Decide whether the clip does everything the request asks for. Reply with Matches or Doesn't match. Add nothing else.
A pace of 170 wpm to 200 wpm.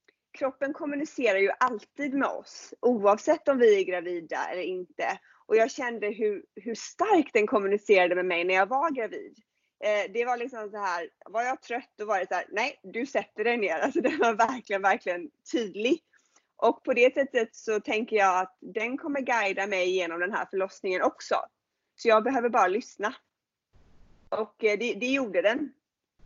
Matches